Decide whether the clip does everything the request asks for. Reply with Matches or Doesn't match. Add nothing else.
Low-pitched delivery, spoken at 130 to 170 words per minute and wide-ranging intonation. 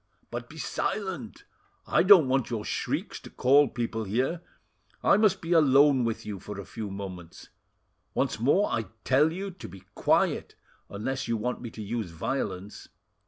Matches